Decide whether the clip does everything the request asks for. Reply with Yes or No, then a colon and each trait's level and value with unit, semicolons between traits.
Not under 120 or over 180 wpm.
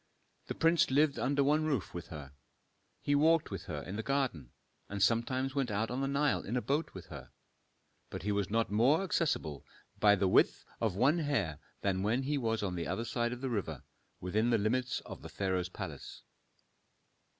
No: average, 195 wpm